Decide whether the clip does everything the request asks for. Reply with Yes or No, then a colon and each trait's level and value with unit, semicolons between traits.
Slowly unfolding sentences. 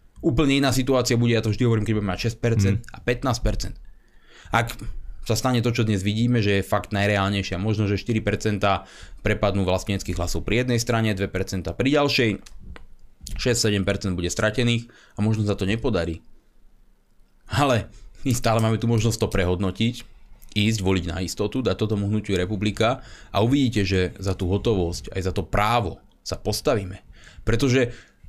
No: average, 155 wpm